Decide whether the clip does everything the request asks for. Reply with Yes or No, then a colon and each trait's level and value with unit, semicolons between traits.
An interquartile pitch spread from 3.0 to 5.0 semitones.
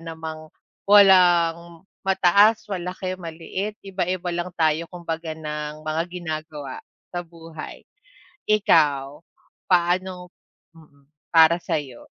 No: narrow, 2.4 semitones